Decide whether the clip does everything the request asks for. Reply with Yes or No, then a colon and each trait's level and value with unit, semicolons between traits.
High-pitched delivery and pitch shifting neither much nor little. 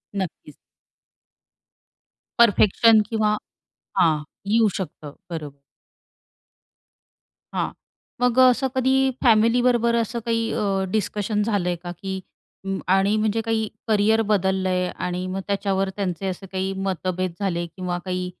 Yes: high, 195 Hz; average, 3.4 semitones